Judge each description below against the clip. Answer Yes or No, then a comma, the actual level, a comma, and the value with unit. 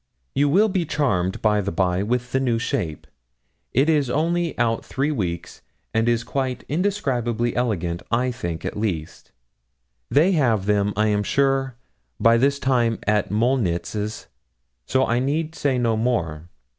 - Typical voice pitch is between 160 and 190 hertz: No, low, 120 Hz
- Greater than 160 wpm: No, average, 155 wpm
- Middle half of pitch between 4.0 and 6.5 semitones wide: Yes, average, 4.7 semitones